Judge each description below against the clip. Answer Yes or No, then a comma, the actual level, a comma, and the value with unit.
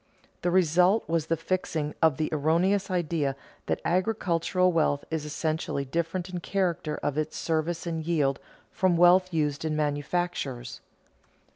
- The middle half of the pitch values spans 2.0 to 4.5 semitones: Yes, average, 2.8 semitones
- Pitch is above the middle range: No, medium, 165 Hz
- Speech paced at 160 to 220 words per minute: No, average, 145 wpm